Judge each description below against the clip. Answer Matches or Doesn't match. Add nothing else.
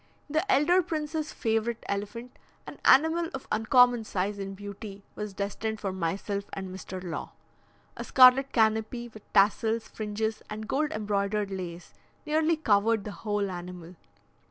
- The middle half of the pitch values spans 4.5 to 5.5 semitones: Doesn't match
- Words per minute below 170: Matches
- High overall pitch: Matches